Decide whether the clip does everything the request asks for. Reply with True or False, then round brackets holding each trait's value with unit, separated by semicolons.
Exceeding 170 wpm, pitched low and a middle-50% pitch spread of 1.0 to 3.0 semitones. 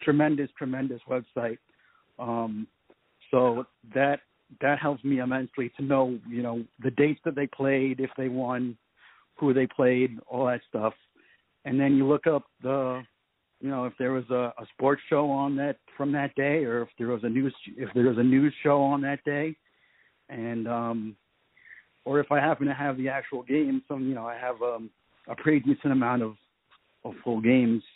True (190 wpm; 130 Hz; 2.5 semitones)